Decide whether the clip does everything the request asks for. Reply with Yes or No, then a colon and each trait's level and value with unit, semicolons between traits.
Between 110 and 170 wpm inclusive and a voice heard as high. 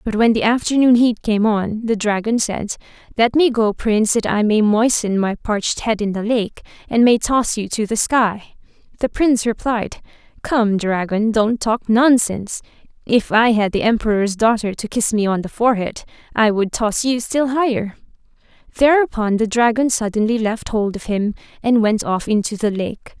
No: average, 185 wpm; high, 220 Hz